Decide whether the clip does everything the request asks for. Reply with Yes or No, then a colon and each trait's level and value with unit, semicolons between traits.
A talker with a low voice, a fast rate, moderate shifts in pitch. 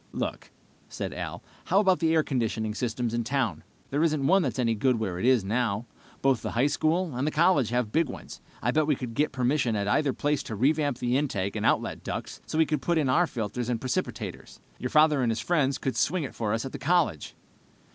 Yes: low, 130 Hz; fast, 230 wpm; average, 4.7 semitones